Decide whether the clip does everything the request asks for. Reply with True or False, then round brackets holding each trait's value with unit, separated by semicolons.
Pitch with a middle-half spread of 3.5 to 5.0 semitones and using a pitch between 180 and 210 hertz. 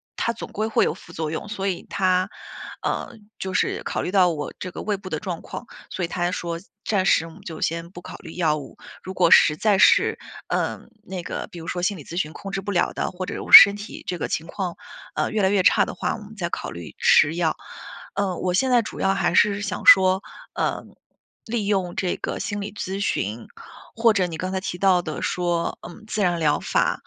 False (2.8 semitones; 185 Hz)